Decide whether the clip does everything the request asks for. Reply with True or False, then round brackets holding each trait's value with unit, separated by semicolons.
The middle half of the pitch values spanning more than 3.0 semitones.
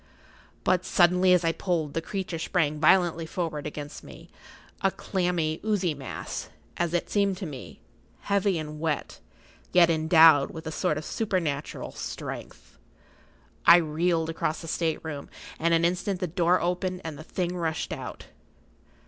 False (2.5 semitones)